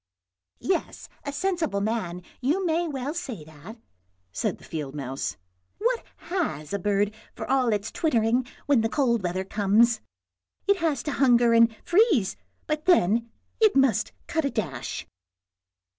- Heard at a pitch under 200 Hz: No, high, 235 Hz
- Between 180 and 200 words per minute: No, average, 160 wpm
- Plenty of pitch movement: Yes, wide, 7.7 semitones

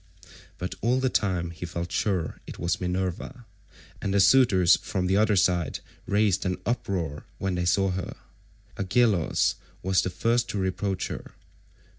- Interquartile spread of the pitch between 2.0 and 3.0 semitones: Yes, narrow, 2.6 semitones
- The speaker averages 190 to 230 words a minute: No, average, 155 wpm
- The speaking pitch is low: Yes, very low, 95 Hz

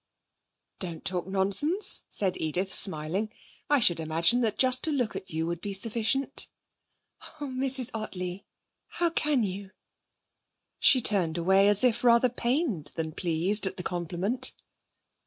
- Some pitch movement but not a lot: No, wide, 5.9 semitones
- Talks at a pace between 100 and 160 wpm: Yes, average, 140 wpm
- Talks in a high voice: Yes, high, 200 Hz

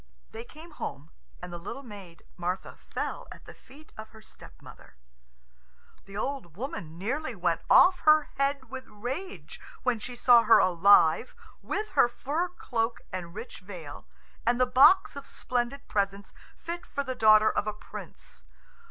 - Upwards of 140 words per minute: Yes, average, 160 wpm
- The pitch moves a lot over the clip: Yes, wide, 5.9 semitones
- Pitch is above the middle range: Yes, high, 235 Hz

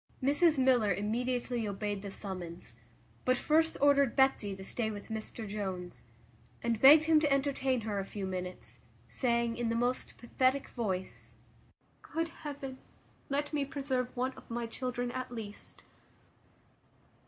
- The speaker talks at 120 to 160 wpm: Yes, average, 140 wpm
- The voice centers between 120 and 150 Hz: No, high, 240 Hz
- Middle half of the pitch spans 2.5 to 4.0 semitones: No, average, 4.8 semitones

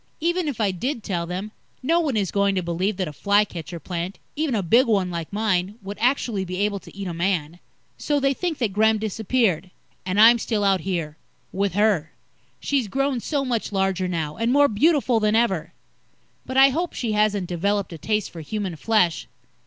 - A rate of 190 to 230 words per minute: Yes, average, 200 wpm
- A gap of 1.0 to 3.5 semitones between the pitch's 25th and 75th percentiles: No, average, 4.6 semitones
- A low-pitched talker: No, high, 205 Hz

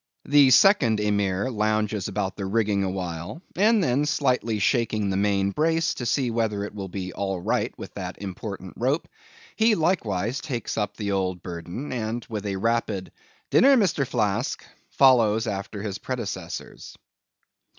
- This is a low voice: Yes, low, 105 Hz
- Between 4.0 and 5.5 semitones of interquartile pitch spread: Yes, average, 4.7 semitones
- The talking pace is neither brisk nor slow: Yes, average, 150 wpm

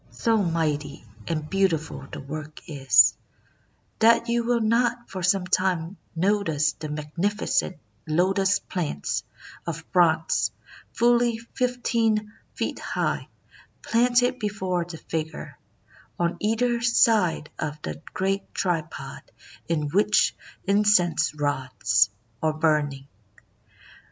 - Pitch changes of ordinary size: No, wide, 5.8 semitones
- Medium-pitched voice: Yes, medium, 180 Hz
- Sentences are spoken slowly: Yes, slow, 105 wpm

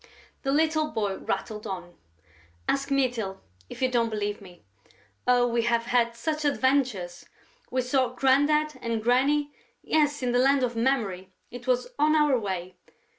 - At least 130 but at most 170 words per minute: Yes, average, 155 wpm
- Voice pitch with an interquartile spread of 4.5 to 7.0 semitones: No, average, 4.1 semitones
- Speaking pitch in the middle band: No, high, 245 Hz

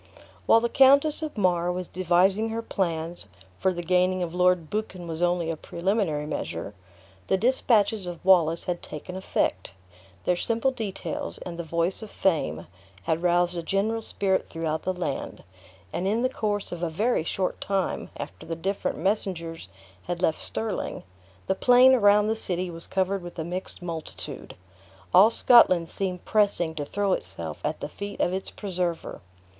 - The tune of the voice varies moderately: Yes, average, 3.3 semitones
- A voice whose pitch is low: No, medium, 180 Hz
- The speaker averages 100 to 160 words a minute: No, average, 170 wpm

